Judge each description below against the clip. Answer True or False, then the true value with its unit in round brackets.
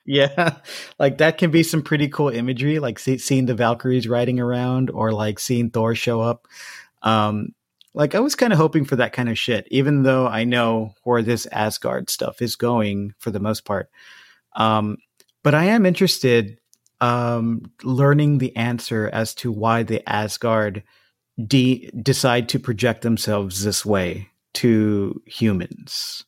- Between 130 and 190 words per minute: True (160 wpm)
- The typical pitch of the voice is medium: False (120 Hz)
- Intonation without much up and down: False (3.4 semitones)